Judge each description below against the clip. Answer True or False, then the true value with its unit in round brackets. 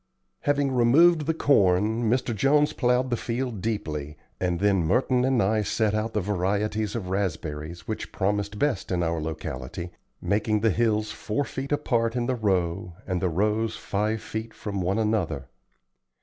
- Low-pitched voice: True (105 Hz)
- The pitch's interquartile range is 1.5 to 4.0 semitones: False (4.5 semitones)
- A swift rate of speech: False (165 wpm)